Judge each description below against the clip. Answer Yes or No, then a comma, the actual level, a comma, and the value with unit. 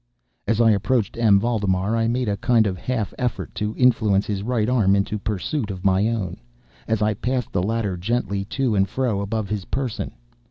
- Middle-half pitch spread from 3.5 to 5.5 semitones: No, average, 3.0 semitones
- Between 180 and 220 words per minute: Yes, average, 195 wpm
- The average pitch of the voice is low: Yes, low, 105 Hz